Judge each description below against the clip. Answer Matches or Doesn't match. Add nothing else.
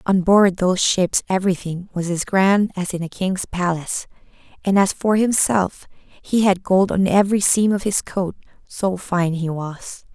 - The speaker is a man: Doesn't match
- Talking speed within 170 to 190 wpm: Matches